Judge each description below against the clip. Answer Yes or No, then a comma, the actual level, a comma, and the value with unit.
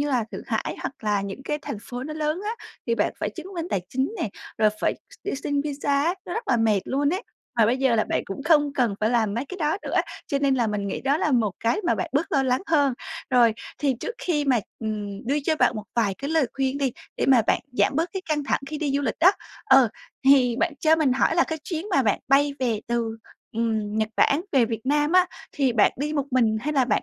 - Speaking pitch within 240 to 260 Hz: No, very high, 270 Hz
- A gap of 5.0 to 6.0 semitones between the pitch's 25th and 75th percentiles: No, average, 4.5 semitones